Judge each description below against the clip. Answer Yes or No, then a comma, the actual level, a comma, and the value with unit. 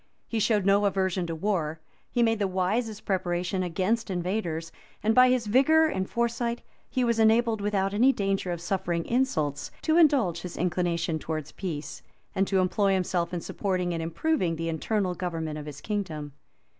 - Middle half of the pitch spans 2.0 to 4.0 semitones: No, average, 4.4 semitones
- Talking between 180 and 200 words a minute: No, average, 170 wpm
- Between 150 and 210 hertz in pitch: Yes, high, 190 Hz